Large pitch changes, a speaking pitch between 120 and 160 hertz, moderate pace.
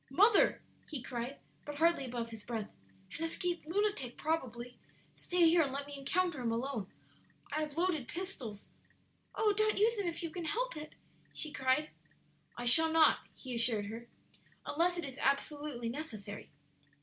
No: wide, 5.9 semitones; very high, 290 Hz; average, 165 wpm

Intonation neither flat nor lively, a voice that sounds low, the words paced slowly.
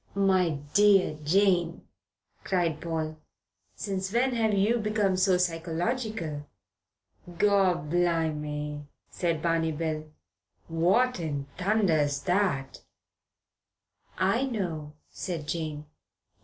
No: average, 4.1 semitones; medium, 175 Hz; slow, 90 wpm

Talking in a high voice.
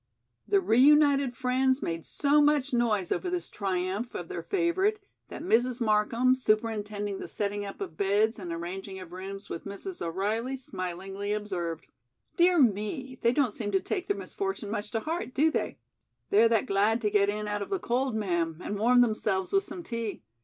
Yes: high, 215 Hz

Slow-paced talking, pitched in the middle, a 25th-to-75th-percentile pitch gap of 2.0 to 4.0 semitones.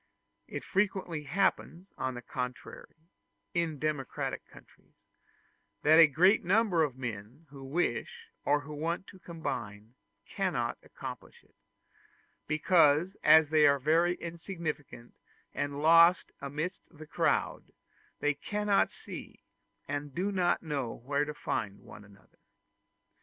Yes: slow, 120 wpm; medium, 155 Hz; average, 3.7 semitones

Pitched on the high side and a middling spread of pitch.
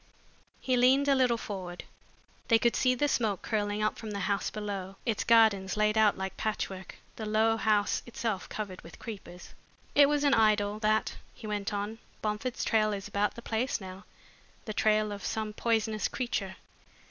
No: high, 215 Hz; narrow, 2.0 semitones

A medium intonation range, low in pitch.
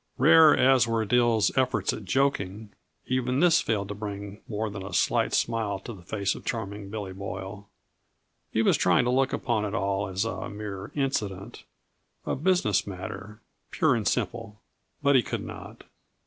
Yes: average, 3.8 semitones; low, 105 Hz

